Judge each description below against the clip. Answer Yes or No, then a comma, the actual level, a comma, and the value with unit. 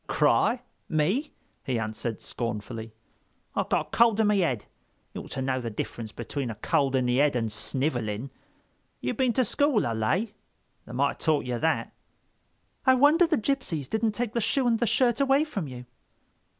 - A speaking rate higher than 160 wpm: Yes, average, 180 wpm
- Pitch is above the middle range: No, medium, 155 Hz